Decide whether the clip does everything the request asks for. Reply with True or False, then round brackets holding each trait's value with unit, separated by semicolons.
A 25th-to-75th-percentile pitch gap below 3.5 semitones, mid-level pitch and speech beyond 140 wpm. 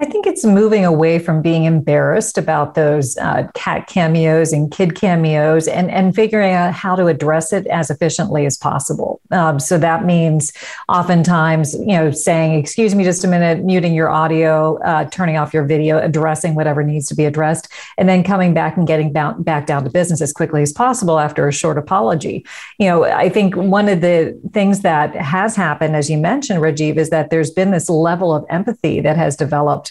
True (2.9 semitones; 165 Hz; 200 wpm)